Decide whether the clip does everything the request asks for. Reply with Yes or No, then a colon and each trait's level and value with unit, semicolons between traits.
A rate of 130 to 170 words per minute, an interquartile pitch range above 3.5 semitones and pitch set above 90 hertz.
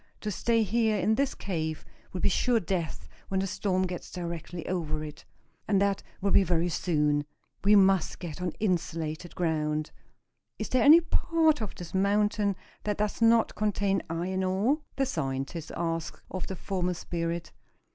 Yes: average, 165 wpm; average, 3.9 semitones; medium, 185 Hz